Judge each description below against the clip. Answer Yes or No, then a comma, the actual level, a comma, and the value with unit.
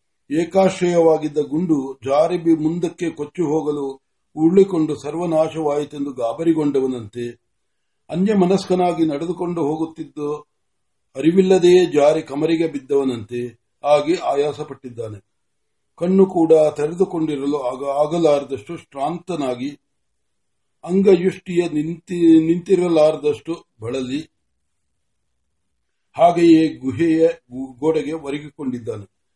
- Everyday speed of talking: No, slow, 60 wpm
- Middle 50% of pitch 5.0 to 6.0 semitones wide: No, average, 3.5 semitones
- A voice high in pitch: No, medium, 155 Hz